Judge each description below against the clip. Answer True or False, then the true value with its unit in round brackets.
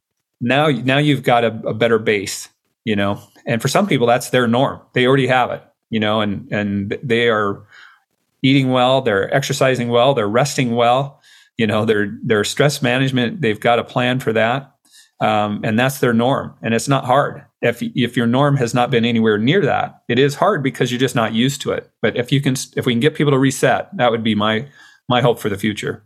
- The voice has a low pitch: True (125 Hz)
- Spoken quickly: True (220 wpm)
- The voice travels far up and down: False (2.9 semitones)